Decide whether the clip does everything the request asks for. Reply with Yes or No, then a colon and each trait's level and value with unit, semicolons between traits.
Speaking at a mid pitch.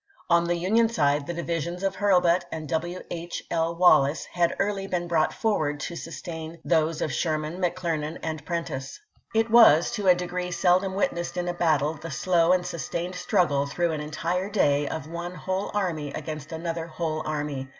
Yes: medium, 170 Hz